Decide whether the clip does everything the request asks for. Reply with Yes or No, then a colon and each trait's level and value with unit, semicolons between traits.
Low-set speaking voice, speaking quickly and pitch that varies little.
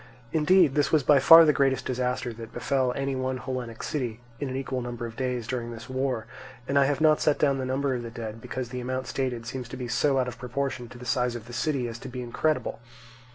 Yes: low, 130 Hz; fast, 240 wpm; narrow, 2.1 semitones